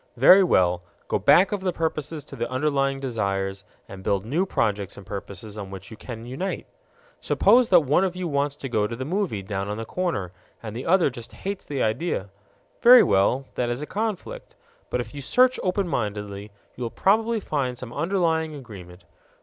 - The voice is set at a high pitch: No, low, 130 Hz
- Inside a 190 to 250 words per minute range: Yes, average, 195 wpm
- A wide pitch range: Yes, wide, 9.0 semitones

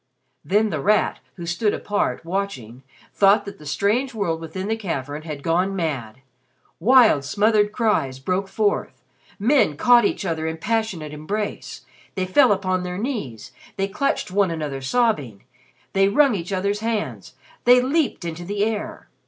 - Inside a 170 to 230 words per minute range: No, average, 155 wpm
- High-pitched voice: Yes, high, 195 Hz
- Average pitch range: Yes, average, 5.0 semitones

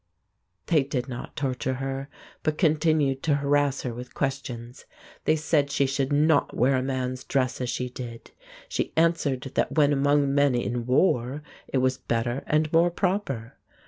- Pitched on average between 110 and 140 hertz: Yes, low, 135 Hz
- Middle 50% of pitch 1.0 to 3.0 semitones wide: Yes, narrow, 2.6 semitones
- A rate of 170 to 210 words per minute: No, average, 160 wpm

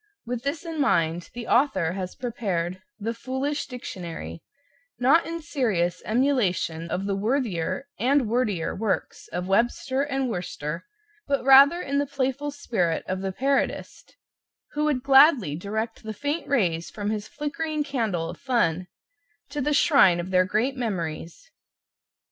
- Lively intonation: Yes, wide, 7.3 semitones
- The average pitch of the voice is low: No, high, 235 Hz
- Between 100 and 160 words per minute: Yes, average, 145 wpm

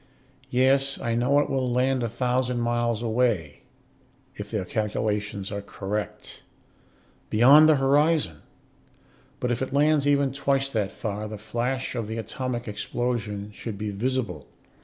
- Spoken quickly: No, average, 140 wpm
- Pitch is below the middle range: Yes, low, 120 Hz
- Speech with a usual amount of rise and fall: Yes, average, 4.0 semitones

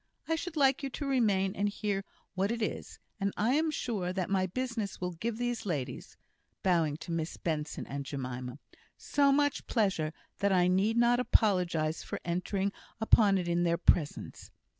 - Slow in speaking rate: No, average, 175 wpm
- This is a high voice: Yes, high, 195 Hz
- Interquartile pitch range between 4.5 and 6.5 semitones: Yes, wide, 5.6 semitones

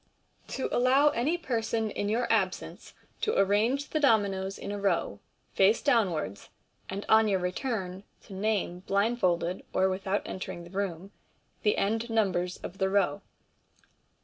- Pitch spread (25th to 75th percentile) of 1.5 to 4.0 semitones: Yes, average, 3.3 semitones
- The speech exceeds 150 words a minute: No, average, 145 wpm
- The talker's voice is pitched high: Yes, high, 200 Hz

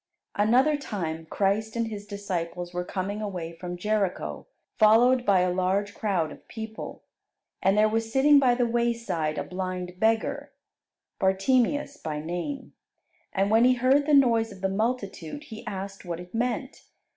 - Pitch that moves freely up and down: No, average, 4.5 semitones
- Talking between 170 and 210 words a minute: No, average, 155 wpm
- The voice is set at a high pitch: Yes, high, 210 Hz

